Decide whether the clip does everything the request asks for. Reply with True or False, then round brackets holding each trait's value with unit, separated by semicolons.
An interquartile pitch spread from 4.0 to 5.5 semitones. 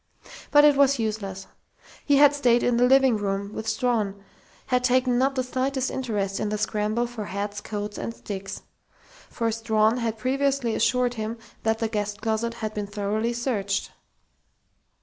False (3.2 semitones)